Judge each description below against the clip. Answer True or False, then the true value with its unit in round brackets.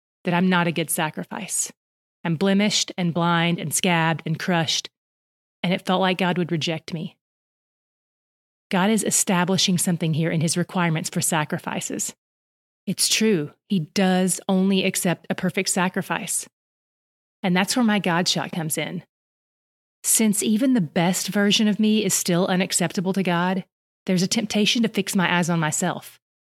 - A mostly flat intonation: True (2.3 semitones)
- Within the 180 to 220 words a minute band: False (160 wpm)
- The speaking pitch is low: False (180 Hz)